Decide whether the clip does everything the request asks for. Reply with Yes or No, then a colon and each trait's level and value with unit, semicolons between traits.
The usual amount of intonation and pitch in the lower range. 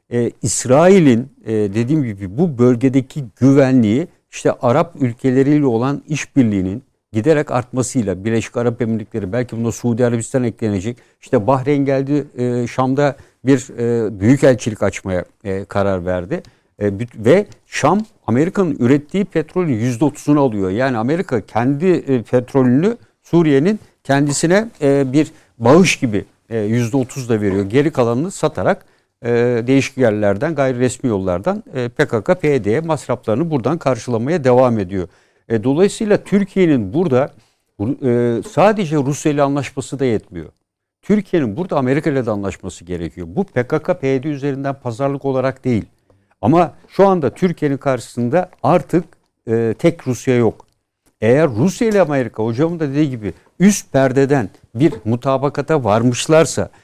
Yes: average, 4.7 semitones; low, 130 Hz